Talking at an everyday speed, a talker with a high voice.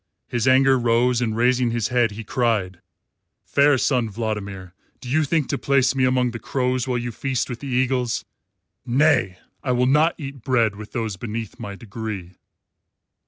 No: average, 170 wpm; low, 120 Hz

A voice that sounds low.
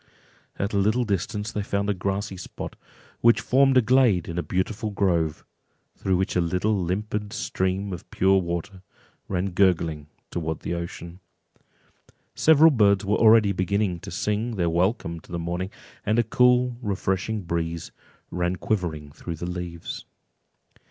Yes: very low, 95 Hz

